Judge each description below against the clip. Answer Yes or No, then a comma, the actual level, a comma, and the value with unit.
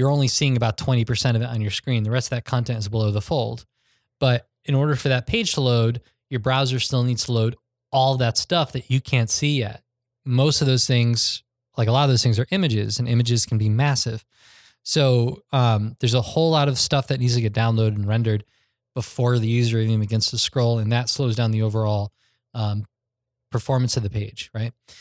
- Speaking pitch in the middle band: No, low, 120 Hz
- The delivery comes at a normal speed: No, fast, 220 wpm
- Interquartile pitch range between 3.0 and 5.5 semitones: No, narrow, 2.5 semitones